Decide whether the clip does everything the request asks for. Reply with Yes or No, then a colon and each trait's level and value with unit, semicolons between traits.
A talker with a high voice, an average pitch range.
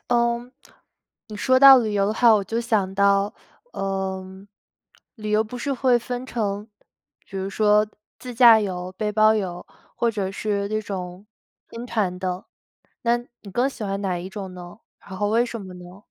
Yes: high, 210 Hz; average, 3.3 semitones